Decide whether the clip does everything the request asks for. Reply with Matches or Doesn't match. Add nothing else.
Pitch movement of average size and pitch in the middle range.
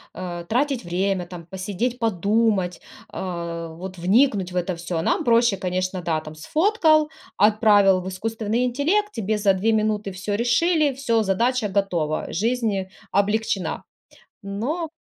Doesn't match